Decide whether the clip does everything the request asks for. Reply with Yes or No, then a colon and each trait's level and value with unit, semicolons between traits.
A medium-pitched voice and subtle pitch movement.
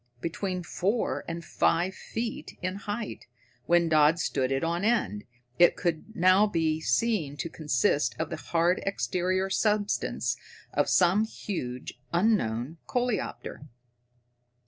No: medium, 175 Hz; average, 4.4 semitones